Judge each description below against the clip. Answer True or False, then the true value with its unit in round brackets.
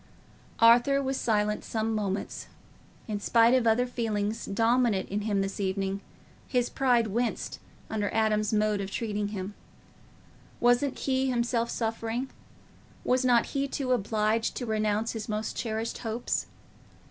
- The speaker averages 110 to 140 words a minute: True (135 wpm)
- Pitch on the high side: True (225 Hz)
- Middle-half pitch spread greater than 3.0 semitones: False (2.5 semitones)